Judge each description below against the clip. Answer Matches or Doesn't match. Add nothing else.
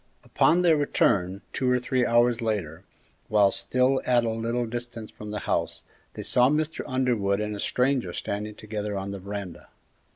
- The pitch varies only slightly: Doesn't match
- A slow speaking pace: Doesn't match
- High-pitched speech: Doesn't match